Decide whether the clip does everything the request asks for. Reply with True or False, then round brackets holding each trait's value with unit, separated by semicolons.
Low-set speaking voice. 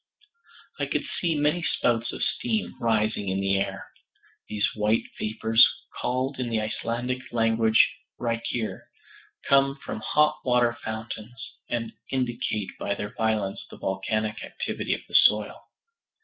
True (115 Hz)